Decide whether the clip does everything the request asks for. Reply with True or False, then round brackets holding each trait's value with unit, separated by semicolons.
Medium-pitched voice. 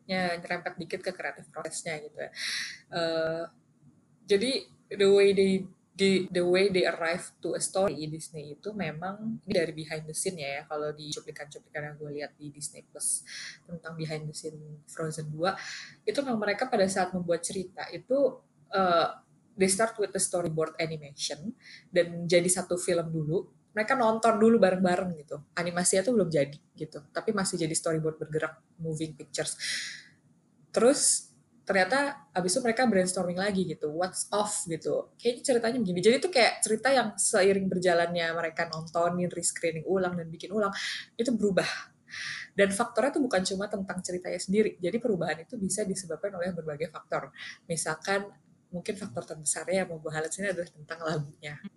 True (180 Hz)